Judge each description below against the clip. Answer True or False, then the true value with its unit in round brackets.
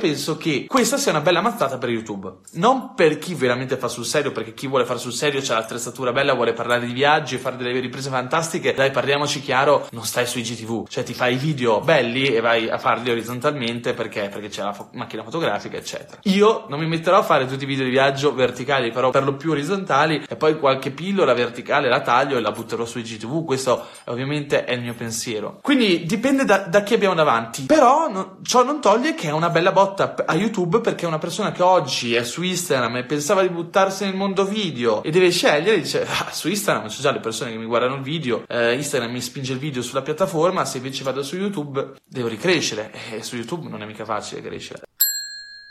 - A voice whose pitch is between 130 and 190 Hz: True (140 Hz)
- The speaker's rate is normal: False (220 wpm)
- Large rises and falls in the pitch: True (6.8 semitones)